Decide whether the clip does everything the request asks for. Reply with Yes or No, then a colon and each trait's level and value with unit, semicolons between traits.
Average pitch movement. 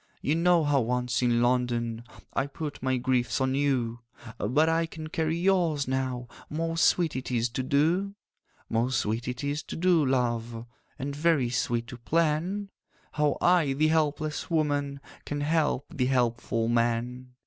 Yes: average, 4.3 semitones